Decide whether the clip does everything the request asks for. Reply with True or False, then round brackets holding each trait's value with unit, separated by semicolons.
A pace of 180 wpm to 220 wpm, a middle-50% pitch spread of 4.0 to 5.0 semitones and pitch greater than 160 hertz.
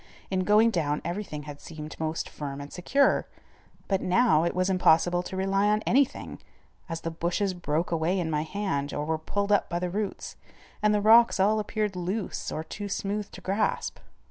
True (190 wpm; 4.3 semitones; 185 Hz)